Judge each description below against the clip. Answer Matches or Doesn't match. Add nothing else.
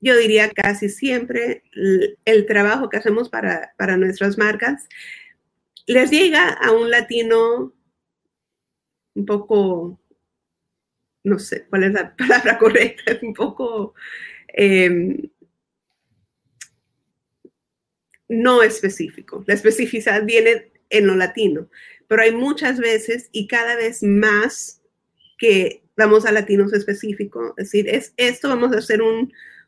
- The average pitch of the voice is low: Doesn't match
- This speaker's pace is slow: Matches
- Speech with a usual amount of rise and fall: Matches